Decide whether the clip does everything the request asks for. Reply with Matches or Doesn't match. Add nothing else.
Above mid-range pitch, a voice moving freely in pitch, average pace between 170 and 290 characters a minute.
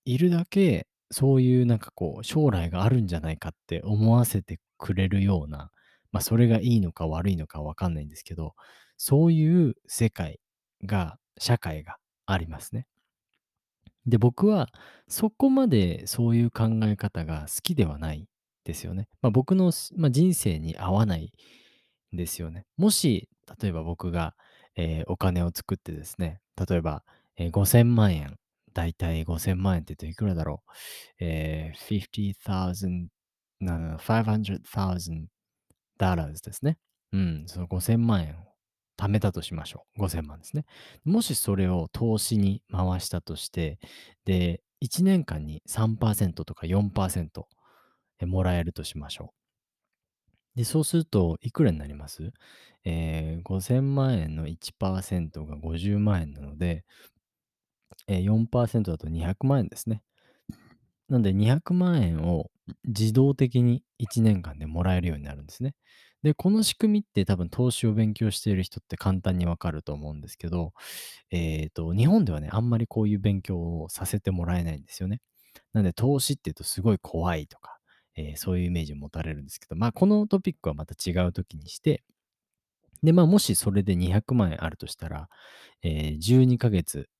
Doesn't match